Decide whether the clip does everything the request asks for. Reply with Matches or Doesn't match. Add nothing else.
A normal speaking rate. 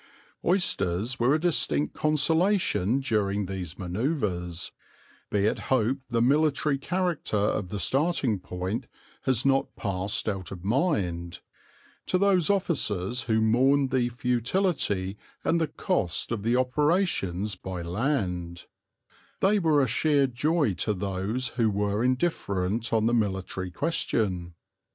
Doesn't match